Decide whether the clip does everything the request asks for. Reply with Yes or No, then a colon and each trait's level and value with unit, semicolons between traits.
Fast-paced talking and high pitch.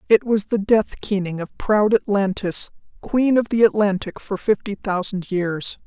No: average, 165 wpm; high, 205 Hz